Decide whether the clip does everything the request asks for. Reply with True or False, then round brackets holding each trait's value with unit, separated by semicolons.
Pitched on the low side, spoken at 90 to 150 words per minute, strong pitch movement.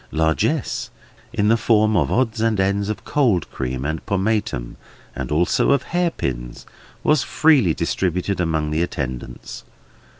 True (95 Hz; 135 wpm; 6.6 semitones)